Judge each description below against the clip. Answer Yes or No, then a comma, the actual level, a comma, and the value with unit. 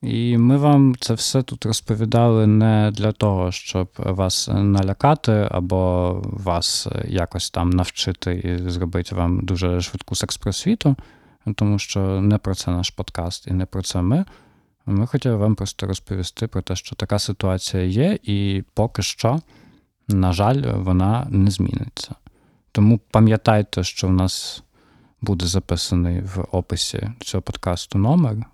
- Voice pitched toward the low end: Yes, low, 100 Hz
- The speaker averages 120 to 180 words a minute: Yes, average, 145 wpm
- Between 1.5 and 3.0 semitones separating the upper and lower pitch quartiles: No, average, 3.5 semitones